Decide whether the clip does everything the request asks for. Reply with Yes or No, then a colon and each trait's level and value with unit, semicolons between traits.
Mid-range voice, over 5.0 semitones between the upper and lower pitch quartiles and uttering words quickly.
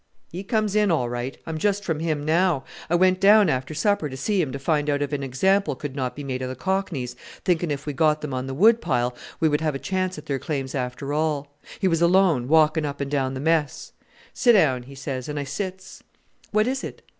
Yes: medium, 150 Hz; wide, 5.4 semitones; fast, 240 wpm